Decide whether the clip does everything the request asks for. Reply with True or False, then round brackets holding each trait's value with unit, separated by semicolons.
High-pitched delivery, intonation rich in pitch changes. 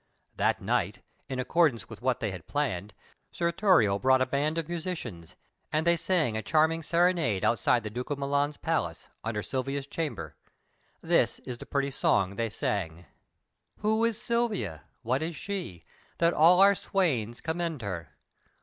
False (140 Hz; 7.3 semitones)